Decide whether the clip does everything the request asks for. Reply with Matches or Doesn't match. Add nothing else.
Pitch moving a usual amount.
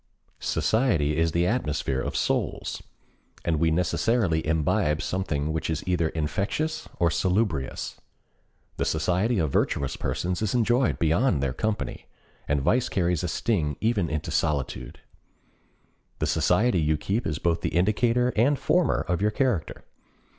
Doesn't match